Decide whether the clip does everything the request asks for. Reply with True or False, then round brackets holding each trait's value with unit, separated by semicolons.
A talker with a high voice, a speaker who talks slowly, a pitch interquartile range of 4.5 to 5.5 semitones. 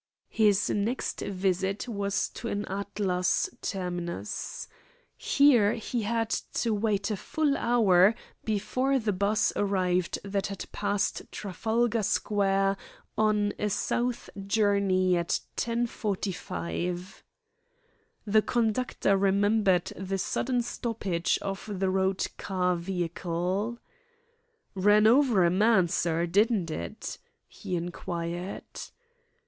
False (200 Hz; 105 wpm; 2.9 semitones)